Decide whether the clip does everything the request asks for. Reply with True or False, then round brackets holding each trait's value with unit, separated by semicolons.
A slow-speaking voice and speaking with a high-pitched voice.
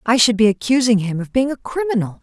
False (240 wpm; 230 Hz)